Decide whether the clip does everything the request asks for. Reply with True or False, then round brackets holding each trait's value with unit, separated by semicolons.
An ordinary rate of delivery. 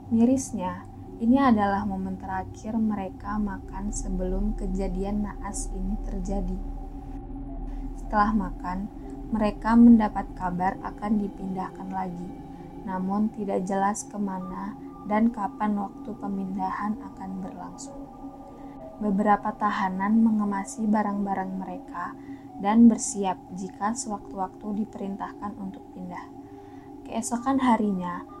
True (95 wpm)